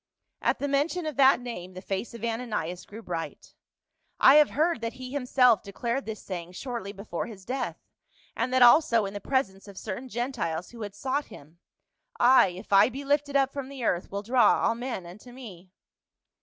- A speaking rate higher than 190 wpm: Yes, average, 200 wpm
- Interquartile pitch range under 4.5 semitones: No, average, 5.1 semitones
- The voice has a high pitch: Yes, high, 235 Hz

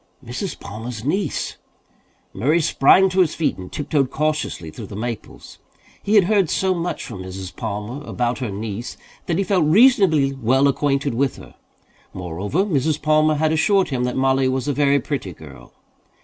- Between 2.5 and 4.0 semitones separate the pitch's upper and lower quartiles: No, wide, 5.5 semitones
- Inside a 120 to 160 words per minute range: No, average, 170 wpm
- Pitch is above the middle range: No, medium, 140 Hz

